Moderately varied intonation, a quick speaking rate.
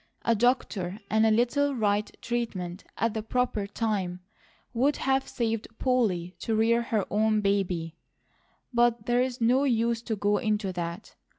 No: average, 3.0 semitones; average, 150 wpm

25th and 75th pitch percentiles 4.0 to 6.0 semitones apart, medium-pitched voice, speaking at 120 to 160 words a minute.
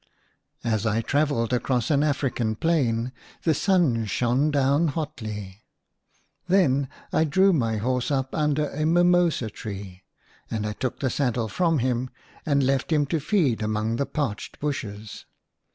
No: average, 5.0 semitones; low, 130 Hz; average, 145 wpm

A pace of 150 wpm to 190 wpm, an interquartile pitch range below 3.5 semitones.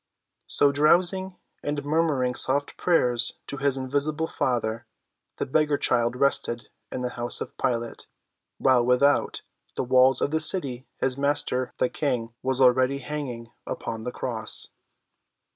No: average, 140 wpm; average, 2.7 semitones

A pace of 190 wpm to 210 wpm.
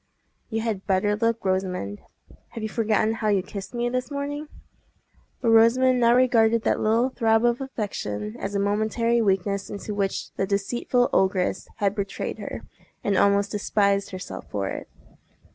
No: average, 160 wpm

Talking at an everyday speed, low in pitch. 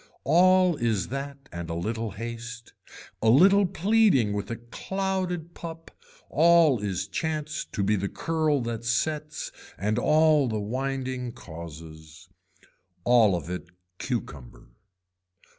No: slow, 125 wpm; low, 125 Hz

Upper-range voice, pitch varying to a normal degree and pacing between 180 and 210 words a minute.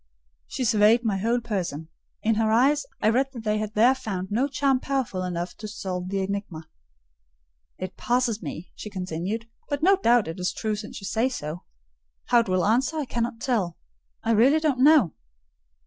Yes: high, 220 Hz; average, 4.9 semitones; average, 185 wpm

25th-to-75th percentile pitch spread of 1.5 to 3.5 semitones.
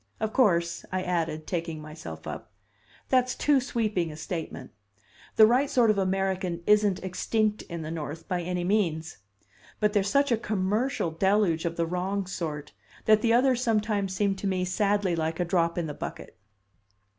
No: average, 4.1 semitones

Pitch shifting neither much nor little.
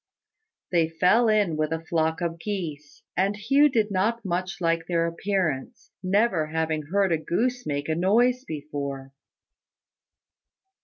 Yes: average, 4.6 semitones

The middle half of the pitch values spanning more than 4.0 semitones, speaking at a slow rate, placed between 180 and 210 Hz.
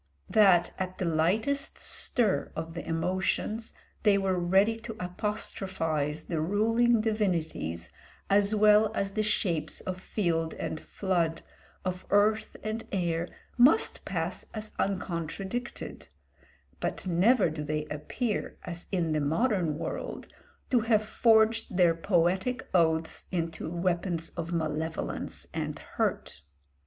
Yes: average, 4.6 semitones; slow, 125 wpm; medium, 185 Hz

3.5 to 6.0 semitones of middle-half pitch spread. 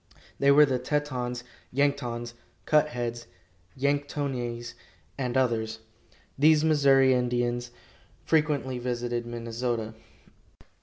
No: average, 2.9 semitones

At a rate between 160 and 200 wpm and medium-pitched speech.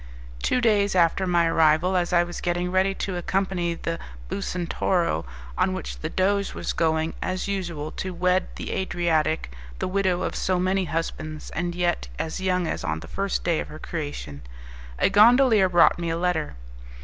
Yes: average, 175 wpm; medium, 175 Hz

